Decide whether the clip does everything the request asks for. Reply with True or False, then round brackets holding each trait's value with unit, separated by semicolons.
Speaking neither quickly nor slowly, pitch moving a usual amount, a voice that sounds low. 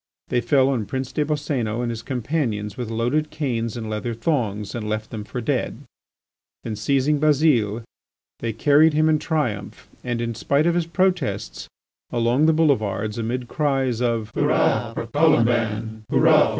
True (155 wpm; 4.7 semitones; 120 Hz)